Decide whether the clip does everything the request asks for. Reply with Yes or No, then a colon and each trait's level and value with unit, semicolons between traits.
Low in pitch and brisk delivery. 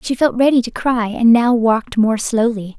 No: high, 235 Hz; fast, 215 wpm